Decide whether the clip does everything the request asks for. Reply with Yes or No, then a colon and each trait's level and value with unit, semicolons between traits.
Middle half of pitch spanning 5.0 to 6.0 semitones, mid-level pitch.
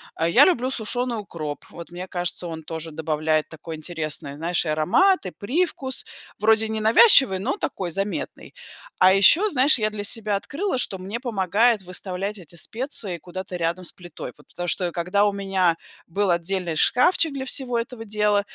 No: average, 5.3 semitones; high, 195 Hz